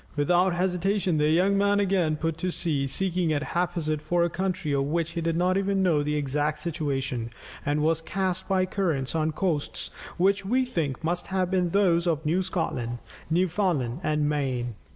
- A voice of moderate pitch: Yes, medium, 170 Hz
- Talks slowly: No, average, 180 wpm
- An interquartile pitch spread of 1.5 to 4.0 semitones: Yes, average, 3.7 semitones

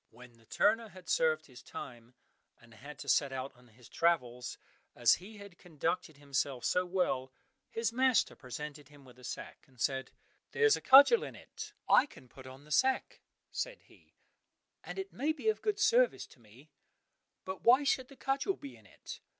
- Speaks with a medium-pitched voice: Yes, medium, 150 Hz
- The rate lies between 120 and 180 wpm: No, average, 190 wpm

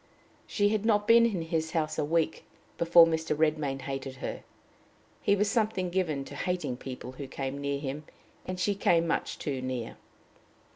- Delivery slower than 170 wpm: No, average, 175 wpm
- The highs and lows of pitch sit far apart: No, average, 4.9 semitones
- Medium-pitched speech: Yes, medium, 160 Hz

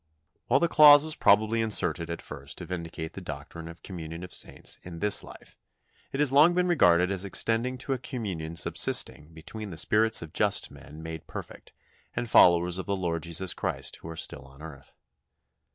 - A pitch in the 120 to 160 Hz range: No, very low, 90 Hz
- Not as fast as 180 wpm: No, average, 195 wpm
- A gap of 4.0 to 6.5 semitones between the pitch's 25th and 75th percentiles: Yes, wide, 5.5 semitones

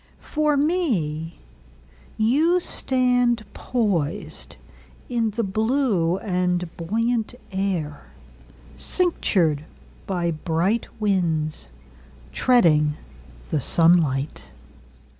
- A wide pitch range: Yes, wide, 7.6 semitones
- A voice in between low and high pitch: Yes, medium, 175 Hz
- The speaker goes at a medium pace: No, slow, 55 wpm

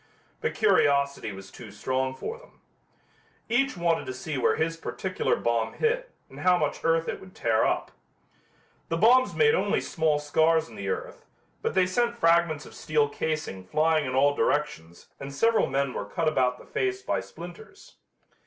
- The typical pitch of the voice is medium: Yes, medium, 155 Hz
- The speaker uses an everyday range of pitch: No, wide, 6.1 semitones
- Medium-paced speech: Yes, average, 175 wpm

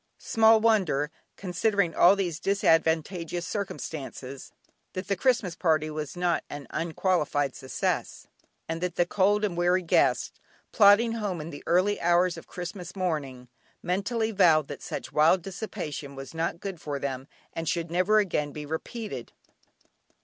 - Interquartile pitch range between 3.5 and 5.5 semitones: Yes, average, 4.3 semitones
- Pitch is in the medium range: Yes, medium, 175 Hz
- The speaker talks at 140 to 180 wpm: Yes, average, 145 wpm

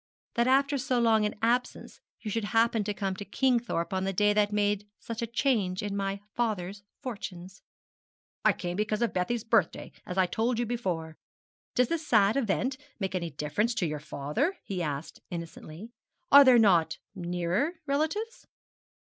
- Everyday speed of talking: Yes, average, 170 wpm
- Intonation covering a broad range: No, average, 4.7 semitones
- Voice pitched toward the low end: No, high, 210 Hz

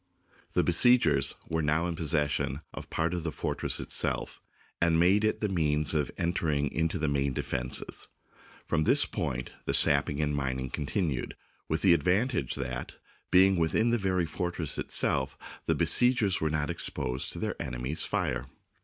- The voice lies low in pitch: Yes, very low, 80 Hz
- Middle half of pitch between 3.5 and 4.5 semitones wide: Yes, average, 3.9 semitones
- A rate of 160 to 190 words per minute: Yes, average, 170 wpm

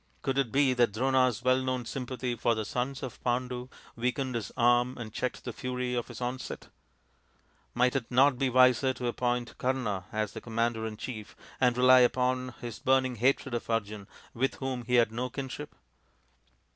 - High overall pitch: No, low, 125 Hz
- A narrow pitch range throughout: Yes, narrow, 1.4 semitones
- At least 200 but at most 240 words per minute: No, average, 175 wpm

